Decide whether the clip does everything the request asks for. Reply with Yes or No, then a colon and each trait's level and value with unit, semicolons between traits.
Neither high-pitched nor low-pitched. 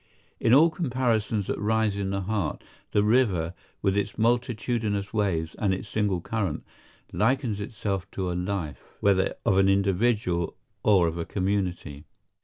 No: low, 100 Hz